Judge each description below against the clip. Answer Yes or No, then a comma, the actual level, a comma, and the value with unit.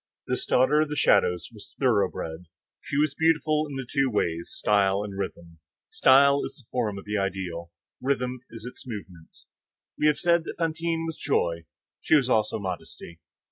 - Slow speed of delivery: No, average, 170 wpm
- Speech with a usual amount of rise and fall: No, wide, 7.4 semitones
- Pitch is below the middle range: Yes, low, 125 Hz